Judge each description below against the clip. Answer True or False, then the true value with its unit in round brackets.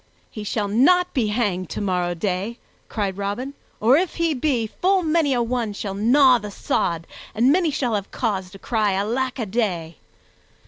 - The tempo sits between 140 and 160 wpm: False (175 wpm)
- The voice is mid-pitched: False (225 Hz)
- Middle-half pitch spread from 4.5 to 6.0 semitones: True (4.8 semitones)